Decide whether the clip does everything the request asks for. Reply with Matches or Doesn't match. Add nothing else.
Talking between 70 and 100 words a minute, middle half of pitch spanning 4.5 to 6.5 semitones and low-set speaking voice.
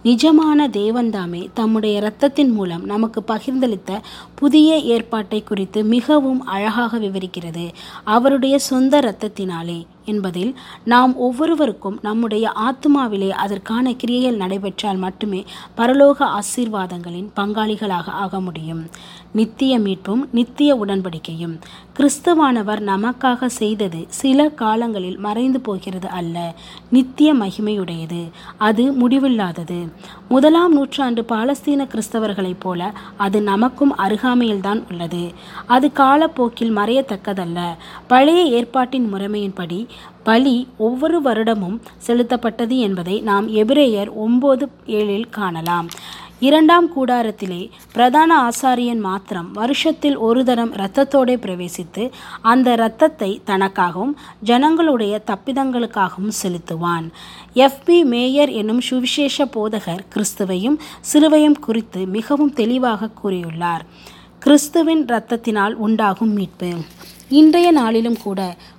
Doesn't match